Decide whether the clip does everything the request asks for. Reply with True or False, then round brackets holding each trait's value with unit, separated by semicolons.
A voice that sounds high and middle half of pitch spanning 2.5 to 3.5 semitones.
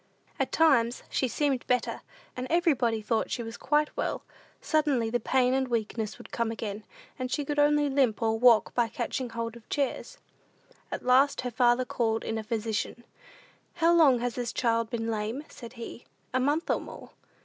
True (245 Hz; 3.2 semitones)